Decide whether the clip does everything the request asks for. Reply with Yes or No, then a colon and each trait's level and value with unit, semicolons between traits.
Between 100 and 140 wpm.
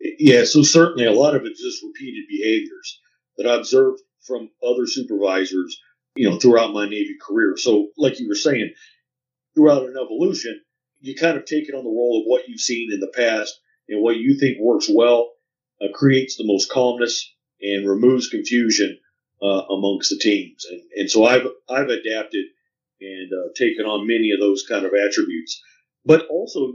No: average, 180 wpm